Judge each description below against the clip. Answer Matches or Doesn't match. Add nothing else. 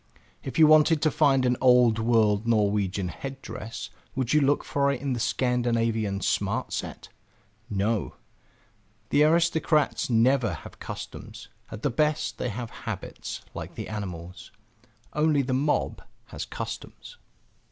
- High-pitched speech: Doesn't match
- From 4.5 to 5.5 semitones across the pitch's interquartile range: Matches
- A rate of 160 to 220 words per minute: Doesn't match